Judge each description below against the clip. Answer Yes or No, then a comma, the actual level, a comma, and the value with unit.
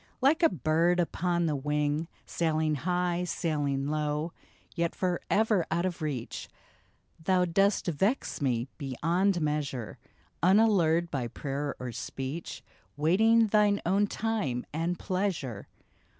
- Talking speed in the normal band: No, slow, 120 wpm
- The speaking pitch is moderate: Yes, medium, 165 Hz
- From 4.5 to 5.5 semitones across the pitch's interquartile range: No, average, 4.0 semitones